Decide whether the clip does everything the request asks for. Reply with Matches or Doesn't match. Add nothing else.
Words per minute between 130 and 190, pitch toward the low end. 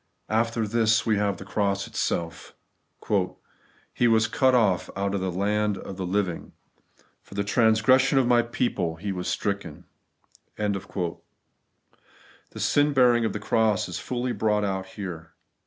Matches